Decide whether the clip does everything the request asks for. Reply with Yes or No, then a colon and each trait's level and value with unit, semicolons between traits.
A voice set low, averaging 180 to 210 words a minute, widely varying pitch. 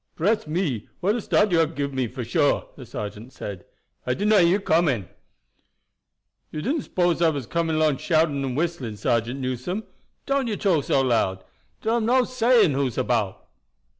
No: medium, 155 Hz; average, 185 wpm; wide, 7.3 semitones